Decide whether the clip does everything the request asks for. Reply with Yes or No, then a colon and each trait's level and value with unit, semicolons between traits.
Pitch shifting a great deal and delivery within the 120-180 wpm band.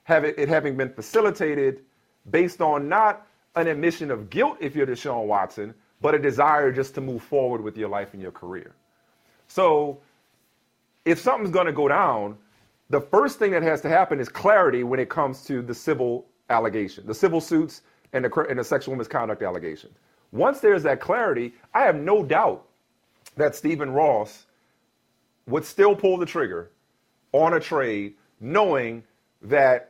Yes: wide, 6.0 semitones; average, 170 wpm